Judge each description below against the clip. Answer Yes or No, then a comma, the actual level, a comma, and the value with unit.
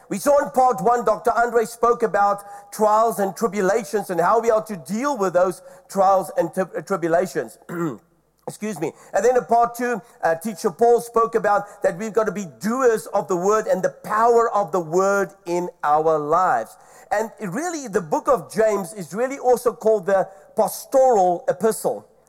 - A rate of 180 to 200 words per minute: Yes, average, 185 wpm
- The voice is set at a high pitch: Yes, high, 210 Hz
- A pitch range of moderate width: Yes, average, 3.7 semitones